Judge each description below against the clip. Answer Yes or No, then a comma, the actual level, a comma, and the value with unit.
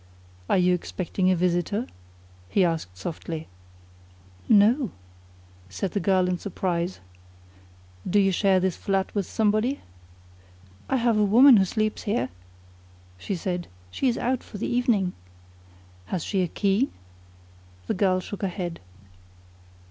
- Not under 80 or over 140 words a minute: Yes, slow, 135 wpm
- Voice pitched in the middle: No, high, 195 Hz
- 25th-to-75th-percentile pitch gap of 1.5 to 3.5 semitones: Yes, average, 3.1 semitones